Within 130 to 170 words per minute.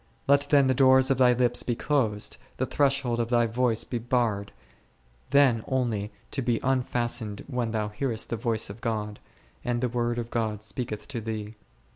No: average, 180 wpm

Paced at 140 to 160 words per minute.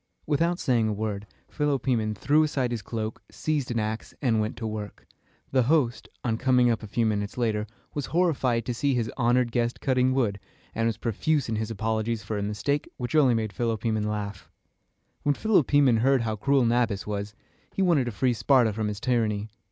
No: average, 190 wpm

